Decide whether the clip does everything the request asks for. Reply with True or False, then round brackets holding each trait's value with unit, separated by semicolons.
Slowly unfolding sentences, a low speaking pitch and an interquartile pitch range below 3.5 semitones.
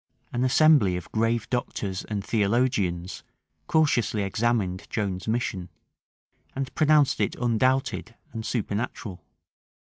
False (100 wpm; 115 Hz; 4.4 semitones)